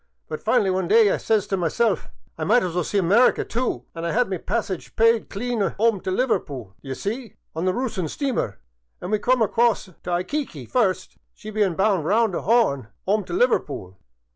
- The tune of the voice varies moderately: Yes, average, 4.7 semitones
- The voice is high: Yes, high, 200 Hz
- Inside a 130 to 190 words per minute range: No, fast, 205 wpm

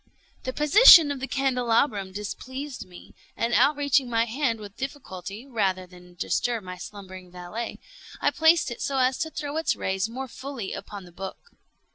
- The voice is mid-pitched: No, high, 235 Hz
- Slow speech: No, average, 165 wpm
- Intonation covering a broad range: Yes, wide, 6.3 semitones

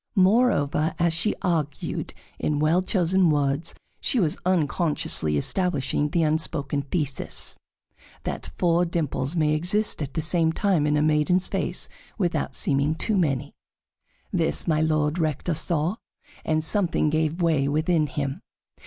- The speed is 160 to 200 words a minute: No, slow, 135 wpm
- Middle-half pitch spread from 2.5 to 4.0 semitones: Yes, average, 2.9 semitones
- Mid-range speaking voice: Yes, medium, 155 Hz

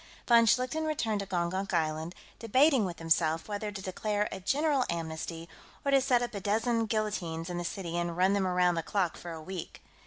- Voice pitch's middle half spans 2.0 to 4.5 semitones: No, average, 4.9 semitones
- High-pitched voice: Yes, high, 195 Hz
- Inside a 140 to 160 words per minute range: No, fast, 205 wpm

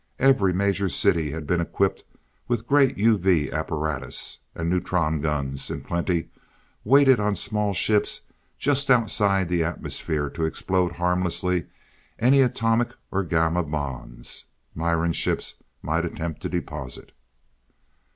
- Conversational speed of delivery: No, slow, 120 wpm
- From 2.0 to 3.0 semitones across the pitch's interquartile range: No, average, 4.6 semitones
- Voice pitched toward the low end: Yes, very low, 90 Hz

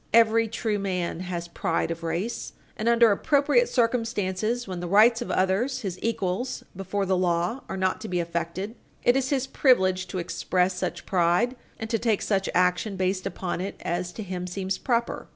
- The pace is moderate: Yes, average, 185 wpm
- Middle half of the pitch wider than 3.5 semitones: Yes, average, 4.1 semitones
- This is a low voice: No, high, 195 Hz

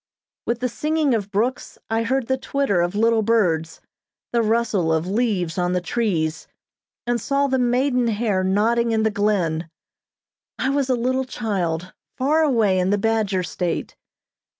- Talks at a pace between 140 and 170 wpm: Yes, average, 160 wpm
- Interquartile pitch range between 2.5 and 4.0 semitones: No, average, 4.9 semitones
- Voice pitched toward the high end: Yes, high, 225 Hz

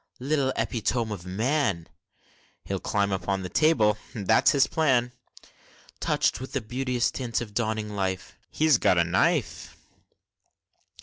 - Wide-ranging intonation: No, average, 4.9 semitones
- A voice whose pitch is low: Yes, low, 110 Hz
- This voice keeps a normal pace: No, slow, 130 wpm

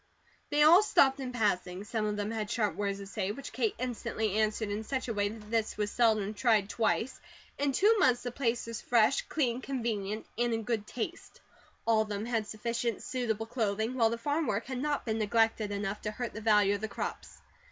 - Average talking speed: No, fast, 215 wpm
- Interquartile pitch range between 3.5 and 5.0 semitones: No, average, 2.7 semitones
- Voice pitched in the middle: No, high, 225 Hz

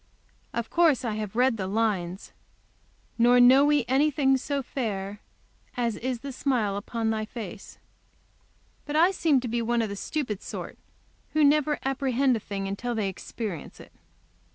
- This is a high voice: Yes, high, 240 Hz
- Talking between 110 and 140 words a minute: No, average, 160 wpm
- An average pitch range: Yes, average, 4.4 semitones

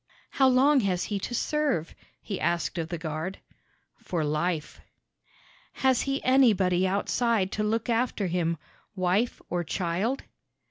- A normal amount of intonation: No, wide, 5.9 semitones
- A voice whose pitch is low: No, high, 195 Hz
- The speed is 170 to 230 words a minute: No, slow, 135 wpm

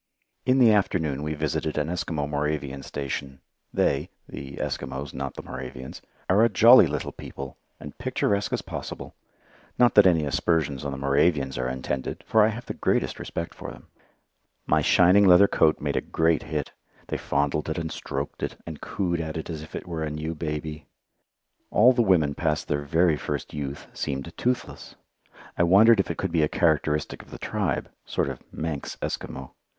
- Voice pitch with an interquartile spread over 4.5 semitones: No, average, 4.0 semitones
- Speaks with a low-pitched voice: Yes, very low, 75 Hz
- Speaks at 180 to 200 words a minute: Yes, average, 185 wpm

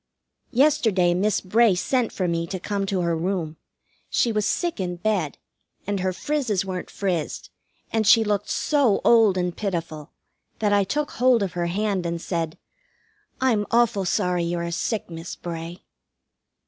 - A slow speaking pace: No, average, 160 wpm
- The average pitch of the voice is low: No, high, 195 Hz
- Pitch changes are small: No, average, 4.0 semitones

